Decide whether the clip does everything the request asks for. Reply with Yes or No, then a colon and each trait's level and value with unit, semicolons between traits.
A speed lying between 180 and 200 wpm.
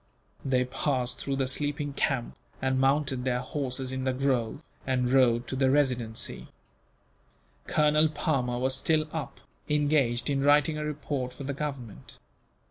No: average, 145 wpm